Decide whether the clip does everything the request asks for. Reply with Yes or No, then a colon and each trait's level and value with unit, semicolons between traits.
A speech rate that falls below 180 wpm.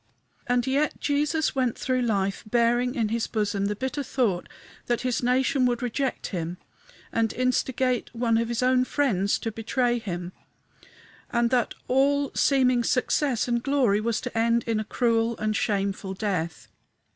Yes: average, 155 wpm